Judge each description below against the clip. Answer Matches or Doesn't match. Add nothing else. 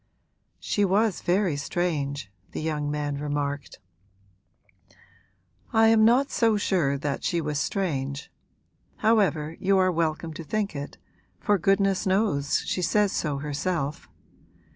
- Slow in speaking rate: Matches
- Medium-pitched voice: Matches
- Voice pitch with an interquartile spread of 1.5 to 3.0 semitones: Doesn't match